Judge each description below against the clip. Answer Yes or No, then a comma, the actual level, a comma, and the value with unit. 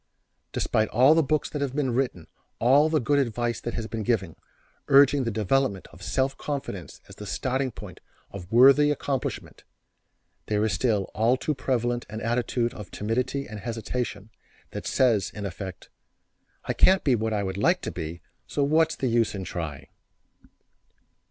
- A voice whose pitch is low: Yes, low, 120 Hz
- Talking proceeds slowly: No, average, 170 wpm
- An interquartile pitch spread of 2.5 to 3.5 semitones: No, average, 4.4 semitones